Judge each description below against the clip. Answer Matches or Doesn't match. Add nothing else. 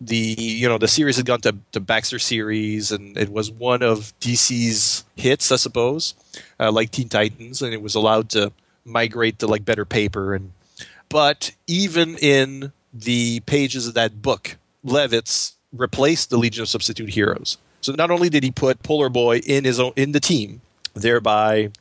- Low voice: Matches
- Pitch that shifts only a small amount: Doesn't match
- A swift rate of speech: Doesn't match